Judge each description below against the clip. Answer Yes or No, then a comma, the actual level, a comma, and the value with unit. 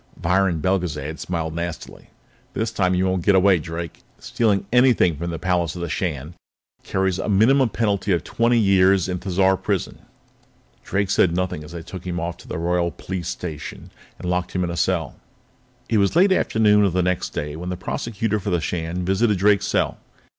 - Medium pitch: No, very low, 90 Hz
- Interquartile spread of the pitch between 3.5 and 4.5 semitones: No, narrow, 2.5 semitones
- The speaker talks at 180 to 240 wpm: Yes, average, 190 wpm